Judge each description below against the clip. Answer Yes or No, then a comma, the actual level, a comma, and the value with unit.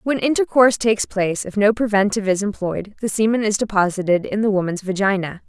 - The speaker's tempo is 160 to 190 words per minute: Yes, average, 185 wpm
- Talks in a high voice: Yes, high, 205 Hz